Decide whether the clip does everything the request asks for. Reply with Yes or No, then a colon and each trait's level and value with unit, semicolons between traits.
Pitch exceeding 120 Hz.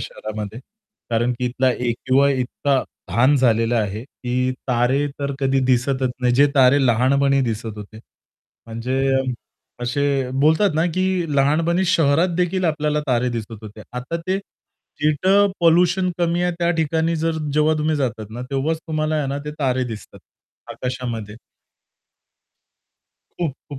Yes: low, 135 Hz